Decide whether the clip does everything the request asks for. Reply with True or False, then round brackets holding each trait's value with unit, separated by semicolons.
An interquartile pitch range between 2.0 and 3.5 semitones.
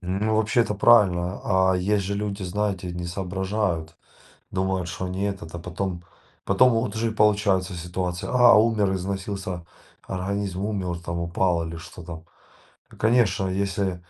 True (2.7 semitones)